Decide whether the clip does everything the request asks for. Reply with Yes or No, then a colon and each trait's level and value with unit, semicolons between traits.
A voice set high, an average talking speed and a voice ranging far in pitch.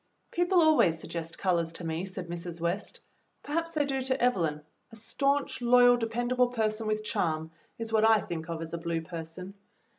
Yes: high, 215 Hz; average, 180 wpm; wide, 6.7 semitones